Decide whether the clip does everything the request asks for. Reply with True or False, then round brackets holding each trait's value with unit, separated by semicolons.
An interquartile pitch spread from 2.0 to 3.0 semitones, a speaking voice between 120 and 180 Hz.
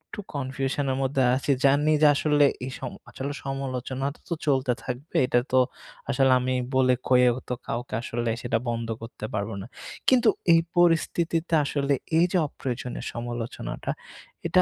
True (2.6 semitones; 135 Hz)